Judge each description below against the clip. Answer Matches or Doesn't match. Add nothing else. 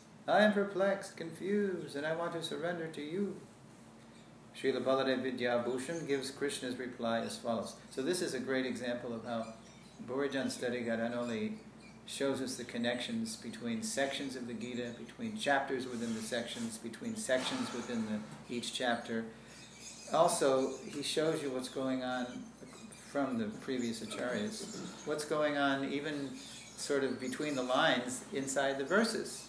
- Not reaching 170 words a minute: Matches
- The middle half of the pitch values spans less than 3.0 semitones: Doesn't match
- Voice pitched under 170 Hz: Matches